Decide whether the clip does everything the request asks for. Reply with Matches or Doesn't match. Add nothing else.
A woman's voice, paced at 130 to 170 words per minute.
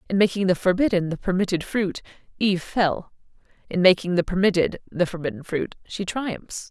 Matches